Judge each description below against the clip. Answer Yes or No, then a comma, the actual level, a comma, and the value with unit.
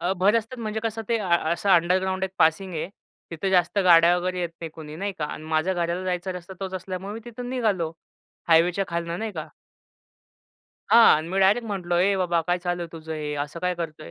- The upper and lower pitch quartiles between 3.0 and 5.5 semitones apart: No, narrow, 2.6 semitones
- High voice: No, medium, 180 Hz